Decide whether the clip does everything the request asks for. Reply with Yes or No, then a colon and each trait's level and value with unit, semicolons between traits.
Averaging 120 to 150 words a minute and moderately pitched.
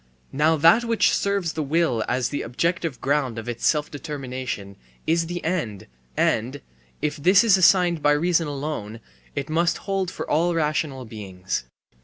No: average, 160 wpm; medium, 150 Hz